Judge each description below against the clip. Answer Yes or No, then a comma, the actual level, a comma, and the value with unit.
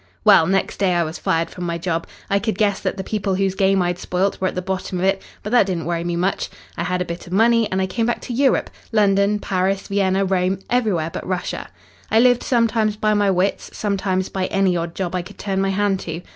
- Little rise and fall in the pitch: Yes, narrow, 2.3 semitones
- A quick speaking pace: Yes, fast, 245 wpm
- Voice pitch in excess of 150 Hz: Yes, high, 190 Hz